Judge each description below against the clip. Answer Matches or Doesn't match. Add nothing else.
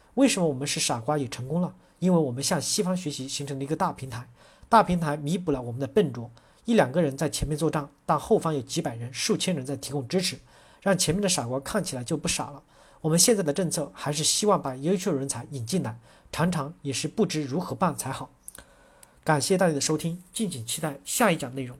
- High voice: Doesn't match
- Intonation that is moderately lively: Matches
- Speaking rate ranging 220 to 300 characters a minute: Doesn't match